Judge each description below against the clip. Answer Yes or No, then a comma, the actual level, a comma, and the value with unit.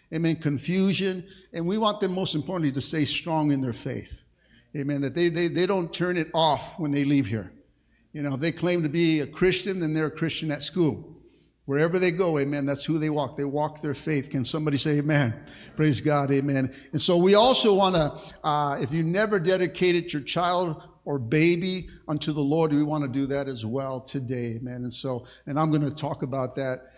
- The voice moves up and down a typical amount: Yes, average, 3.7 semitones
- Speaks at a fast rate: Yes, fast, 215 wpm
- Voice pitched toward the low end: No, medium, 155 Hz